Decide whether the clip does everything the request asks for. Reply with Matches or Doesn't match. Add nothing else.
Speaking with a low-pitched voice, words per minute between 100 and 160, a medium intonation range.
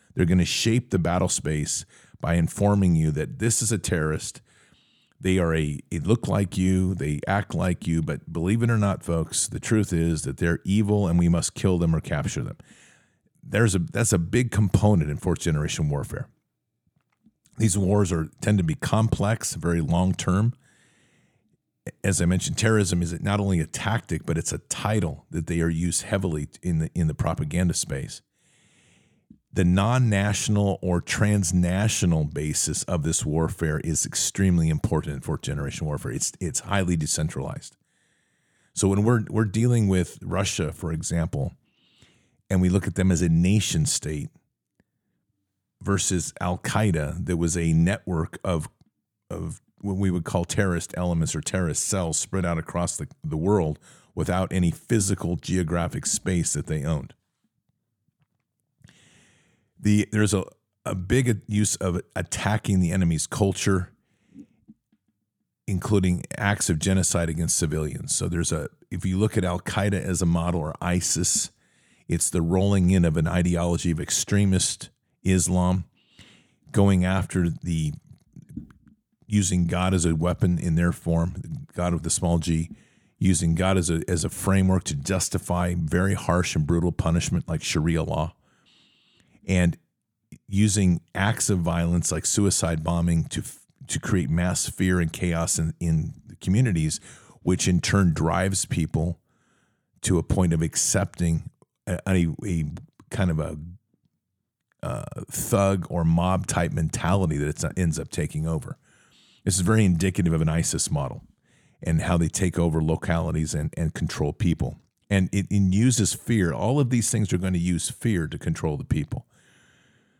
Matches